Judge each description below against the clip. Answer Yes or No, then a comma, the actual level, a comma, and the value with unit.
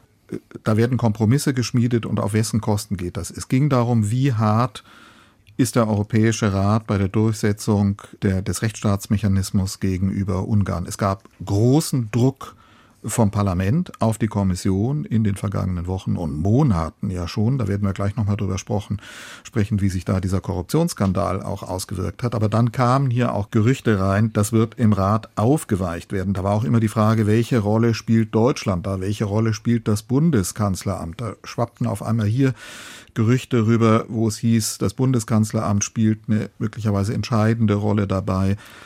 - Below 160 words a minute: No, average, 165 wpm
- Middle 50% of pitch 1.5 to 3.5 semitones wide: Yes, average, 2.7 semitones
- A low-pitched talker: Yes, low, 110 Hz